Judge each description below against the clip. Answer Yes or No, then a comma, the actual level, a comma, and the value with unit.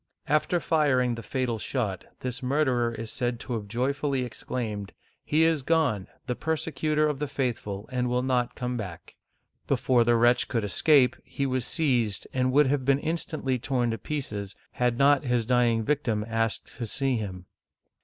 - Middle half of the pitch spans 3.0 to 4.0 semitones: Yes, average, 3.3 semitones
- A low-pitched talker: Yes, low, 125 Hz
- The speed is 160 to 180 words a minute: Yes, average, 175 wpm